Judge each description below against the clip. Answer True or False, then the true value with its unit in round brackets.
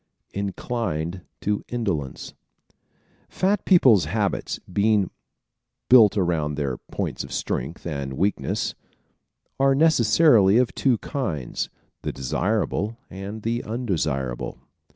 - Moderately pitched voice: False (100 Hz)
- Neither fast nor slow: False (105 wpm)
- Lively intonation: True (7.3 semitones)